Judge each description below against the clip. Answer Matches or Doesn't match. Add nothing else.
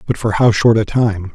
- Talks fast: Matches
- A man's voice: Matches